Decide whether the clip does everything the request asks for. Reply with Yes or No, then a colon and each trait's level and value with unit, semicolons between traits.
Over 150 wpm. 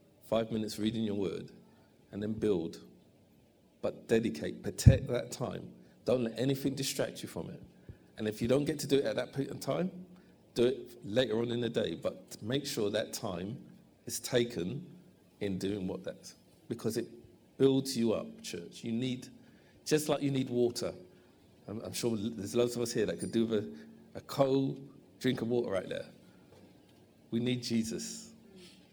Yes: average, 180 wpm